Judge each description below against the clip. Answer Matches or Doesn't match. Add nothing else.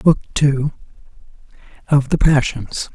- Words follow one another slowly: Matches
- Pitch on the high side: Doesn't match